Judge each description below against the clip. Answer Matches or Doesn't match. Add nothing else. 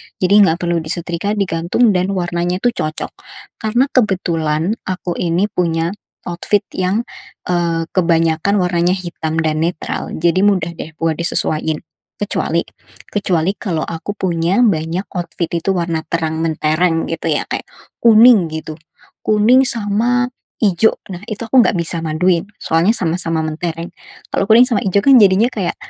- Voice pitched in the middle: Matches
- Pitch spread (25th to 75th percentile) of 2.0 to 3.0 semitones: Doesn't match